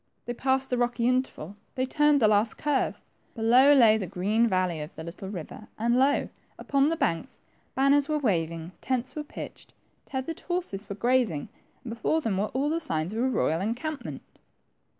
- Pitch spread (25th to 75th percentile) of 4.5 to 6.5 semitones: Yes, wide, 5.6 semitones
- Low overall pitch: No, high, 240 Hz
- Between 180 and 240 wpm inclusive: Yes, average, 185 wpm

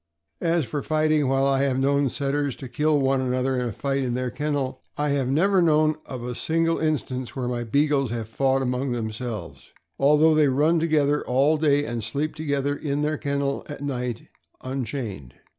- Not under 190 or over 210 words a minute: Yes, average, 195 wpm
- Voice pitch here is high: No, medium, 140 Hz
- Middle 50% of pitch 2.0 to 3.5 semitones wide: Yes, average, 2.7 semitones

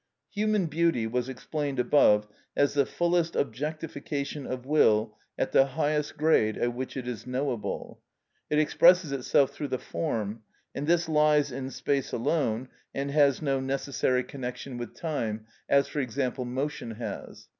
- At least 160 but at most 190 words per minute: No, average, 150 wpm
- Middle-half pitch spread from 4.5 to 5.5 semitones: No, average, 3.4 semitones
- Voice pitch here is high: No, medium, 140 Hz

